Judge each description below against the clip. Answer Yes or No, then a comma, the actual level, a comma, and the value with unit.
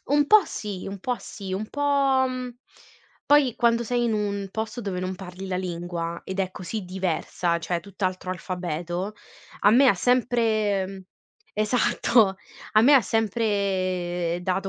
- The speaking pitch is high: Yes, high, 200 Hz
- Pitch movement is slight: No, average, 4.2 semitones